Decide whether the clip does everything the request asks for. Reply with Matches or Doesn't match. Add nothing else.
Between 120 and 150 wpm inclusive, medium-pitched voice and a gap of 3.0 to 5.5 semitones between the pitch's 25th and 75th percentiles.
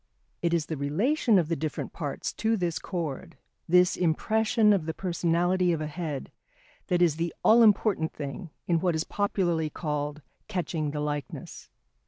Doesn't match